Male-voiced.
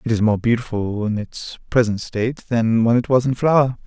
Yes: male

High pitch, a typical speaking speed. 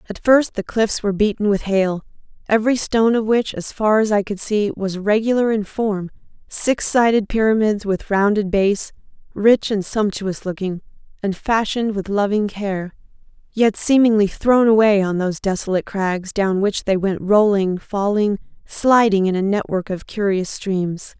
Yes: high, 205 Hz; average, 165 wpm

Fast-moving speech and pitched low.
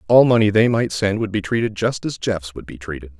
Yes: fast, 265 wpm; low, 105 Hz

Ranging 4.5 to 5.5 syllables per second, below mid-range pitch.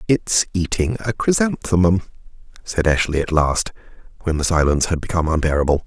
No: 5.8 syllables/s; very low, 85 Hz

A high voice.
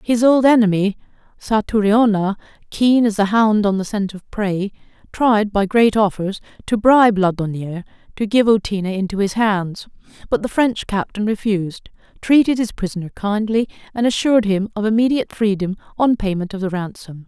Yes: high, 210 Hz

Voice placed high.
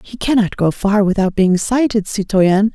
Yes: high, 205 Hz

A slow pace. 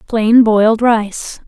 Yes: slow, 120 wpm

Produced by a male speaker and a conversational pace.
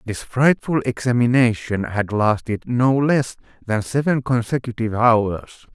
No: male; slow, 115 wpm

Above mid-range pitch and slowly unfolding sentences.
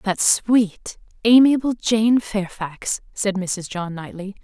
Yes: high, 205 Hz; slow, 120 wpm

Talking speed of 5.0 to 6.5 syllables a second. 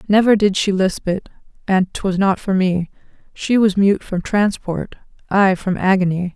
No: 4.6 syllables/s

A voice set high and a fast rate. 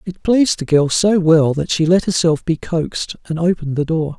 No: medium, 165 Hz; fast, 230 wpm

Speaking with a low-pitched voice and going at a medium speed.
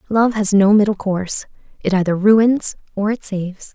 No: high, 205 Hz; average, 175 wpm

